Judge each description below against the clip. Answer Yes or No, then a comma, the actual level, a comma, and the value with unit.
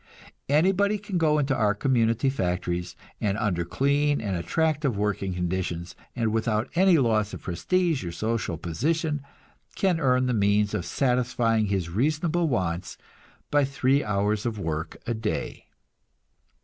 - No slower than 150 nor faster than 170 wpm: No, slow, 135 wpm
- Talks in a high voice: No, low, 115 Hz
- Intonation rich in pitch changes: Yes, wide, 6.8 semitones